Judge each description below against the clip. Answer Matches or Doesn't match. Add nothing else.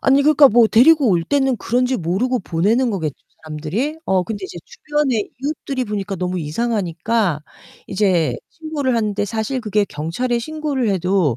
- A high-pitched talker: Matches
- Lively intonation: Matches